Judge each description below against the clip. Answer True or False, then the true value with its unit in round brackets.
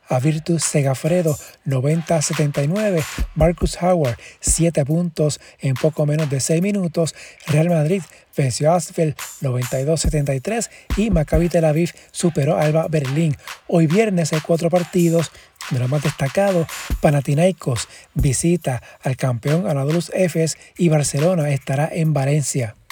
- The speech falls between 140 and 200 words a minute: False (125 wpm)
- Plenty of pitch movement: False (2.9 semitones)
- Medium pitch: True (160 Hz)